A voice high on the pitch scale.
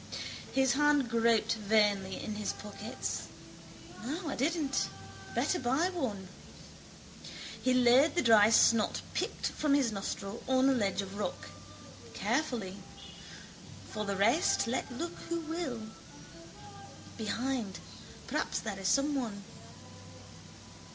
Yes: high, 240 Hz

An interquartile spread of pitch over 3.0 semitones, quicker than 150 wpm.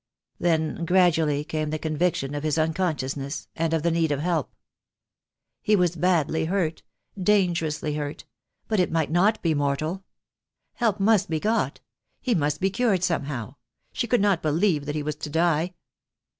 Yes: average, 3.5 semitones; average, 170 wpm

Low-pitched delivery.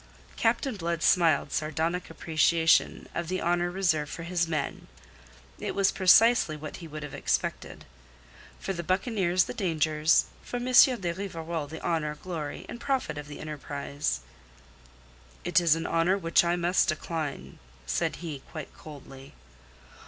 No: medium, 165 Hz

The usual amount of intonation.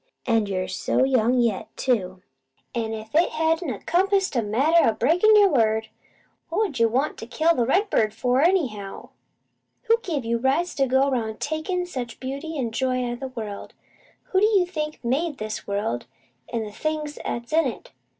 No: wide, 6.3 semitones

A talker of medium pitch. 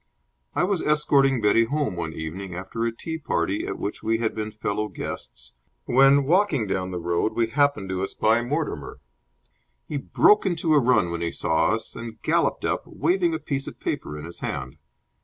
No: low, 115 Hz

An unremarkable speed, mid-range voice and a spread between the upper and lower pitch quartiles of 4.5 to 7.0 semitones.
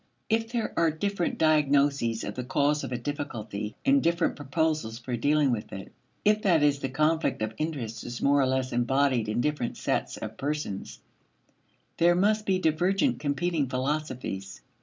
Yes: average, 165 wpm; medium, 145 Hz; average, 4.9 semitones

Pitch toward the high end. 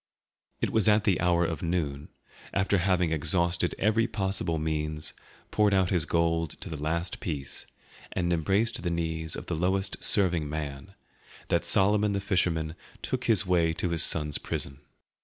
No: very low, 85 Hz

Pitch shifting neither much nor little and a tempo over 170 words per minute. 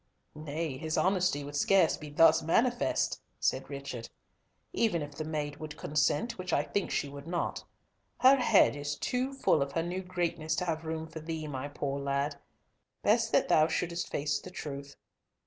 Yes: average, 3.5 semitones; average, 180 wpm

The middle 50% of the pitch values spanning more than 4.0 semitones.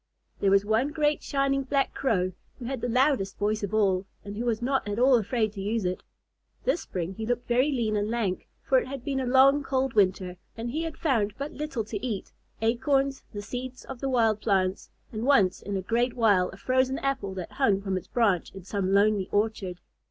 Yes: average, 4.9 semitones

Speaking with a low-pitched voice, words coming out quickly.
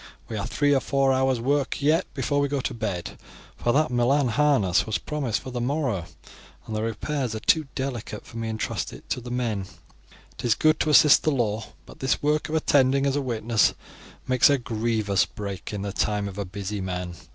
Yes: low, 120 Hz; fast, 215 wpm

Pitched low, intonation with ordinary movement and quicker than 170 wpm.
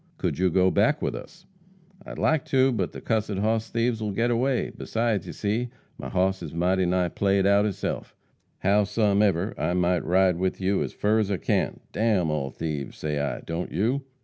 Yes: low, 100 Hz; average, 3.5 semitones; average, 200 wpm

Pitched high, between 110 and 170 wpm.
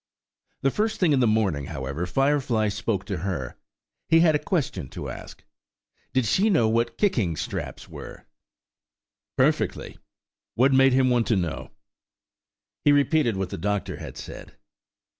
No: low, 115 Hz; average, 150 wpm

